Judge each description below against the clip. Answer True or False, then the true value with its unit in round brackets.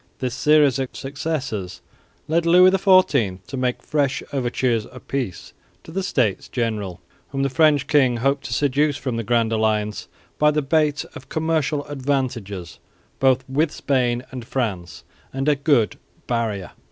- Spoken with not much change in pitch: False (4.2 semitones)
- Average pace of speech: True (155 wpm)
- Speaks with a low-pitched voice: True (130 Hz)